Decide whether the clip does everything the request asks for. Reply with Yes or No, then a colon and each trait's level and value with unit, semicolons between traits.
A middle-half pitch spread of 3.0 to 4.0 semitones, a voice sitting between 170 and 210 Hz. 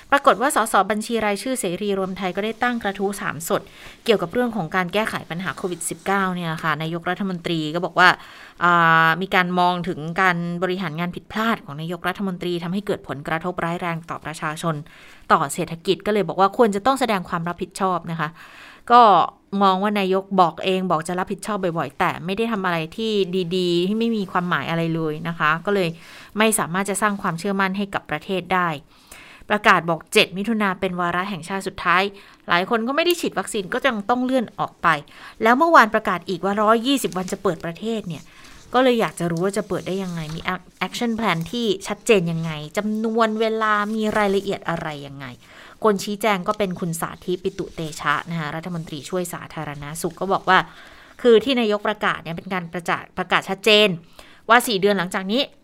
Yes: average, 3.6 semitones; medium, 185 Hz